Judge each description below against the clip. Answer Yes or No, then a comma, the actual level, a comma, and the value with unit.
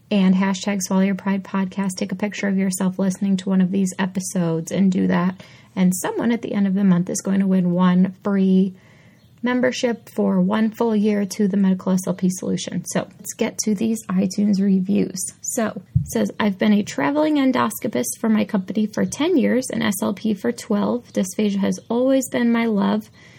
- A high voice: Yes, high, 200 Hz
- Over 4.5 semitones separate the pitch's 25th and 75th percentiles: No, narrow, 2.5 semitones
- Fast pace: No, average, 190 wpm